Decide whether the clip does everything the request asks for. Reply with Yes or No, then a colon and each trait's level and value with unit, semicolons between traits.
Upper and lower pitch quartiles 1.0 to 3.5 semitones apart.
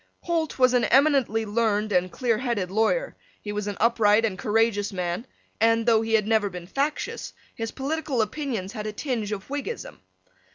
No: average, 3.9 semitones